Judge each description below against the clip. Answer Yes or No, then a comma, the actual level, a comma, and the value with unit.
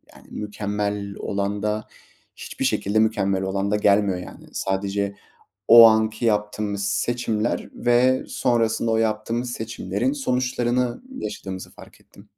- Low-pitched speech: Yes, low, 105 Hz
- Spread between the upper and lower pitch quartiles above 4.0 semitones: No, average, 2.7 semitones